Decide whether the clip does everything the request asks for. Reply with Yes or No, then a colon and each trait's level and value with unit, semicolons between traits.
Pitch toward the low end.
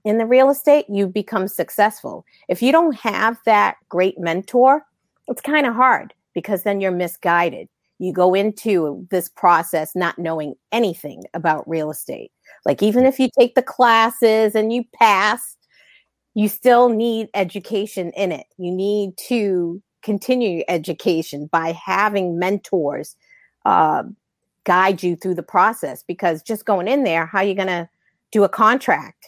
No: high, 200 Hz